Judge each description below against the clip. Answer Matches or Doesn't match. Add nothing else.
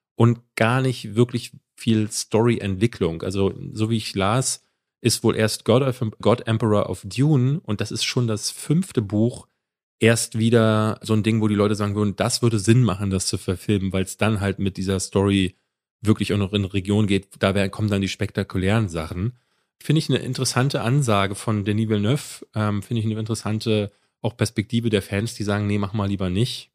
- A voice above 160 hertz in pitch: Doesn't match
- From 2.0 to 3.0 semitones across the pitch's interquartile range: Matches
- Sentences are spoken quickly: Matches